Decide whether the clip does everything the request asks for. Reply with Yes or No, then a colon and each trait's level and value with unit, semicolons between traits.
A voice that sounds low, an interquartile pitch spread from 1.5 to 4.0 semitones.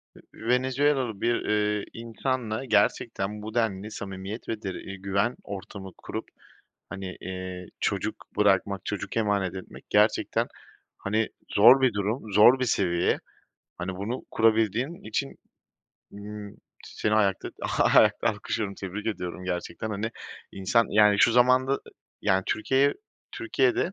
Yes: low, 105 Hz; average, 3.1 semitones